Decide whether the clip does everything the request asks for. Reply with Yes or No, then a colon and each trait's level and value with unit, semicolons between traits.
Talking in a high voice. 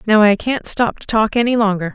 Yes: high, 215 Hz